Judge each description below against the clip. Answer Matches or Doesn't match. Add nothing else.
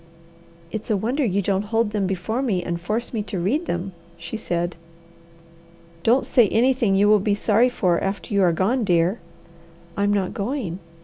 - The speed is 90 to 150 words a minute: Doesn't match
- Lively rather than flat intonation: Doesn't match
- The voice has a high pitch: Matches